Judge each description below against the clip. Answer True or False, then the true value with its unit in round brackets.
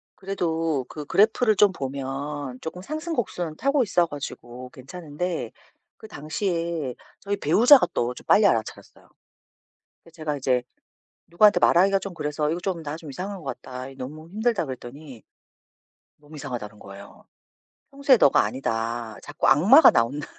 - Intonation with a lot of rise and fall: True (6.5 semitones)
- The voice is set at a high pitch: False (155 Hz)